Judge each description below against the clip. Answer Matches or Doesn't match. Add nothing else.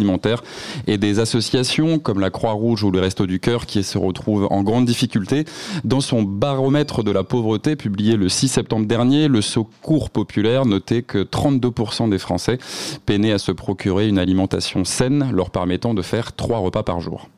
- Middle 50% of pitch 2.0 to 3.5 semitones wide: Doesn't match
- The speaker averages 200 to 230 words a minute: Doesn't match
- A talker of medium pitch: Doesn't match